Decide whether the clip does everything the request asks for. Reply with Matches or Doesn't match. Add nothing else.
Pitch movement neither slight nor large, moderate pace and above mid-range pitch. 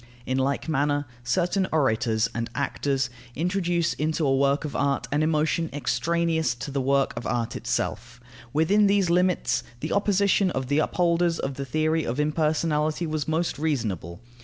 Doesn't match